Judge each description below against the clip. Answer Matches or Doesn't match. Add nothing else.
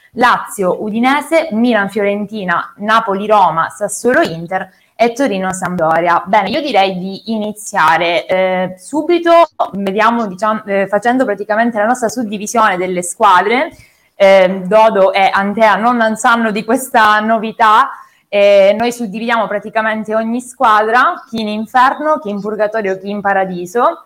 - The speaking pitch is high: Matches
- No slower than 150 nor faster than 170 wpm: Doesn't match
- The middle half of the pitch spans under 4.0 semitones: Matches